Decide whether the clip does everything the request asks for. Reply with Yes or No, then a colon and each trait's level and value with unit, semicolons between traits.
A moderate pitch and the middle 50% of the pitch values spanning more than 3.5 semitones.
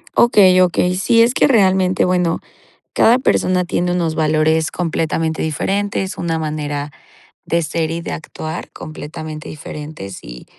No: medium, 165 Hz; average, 2.9 semitones